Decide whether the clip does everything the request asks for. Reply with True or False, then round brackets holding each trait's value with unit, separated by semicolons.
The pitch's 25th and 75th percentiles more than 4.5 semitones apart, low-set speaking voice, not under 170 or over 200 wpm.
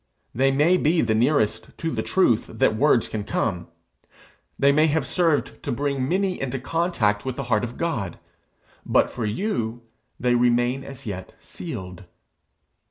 False (5.3 semitones; 130 Hz; 160 wpm)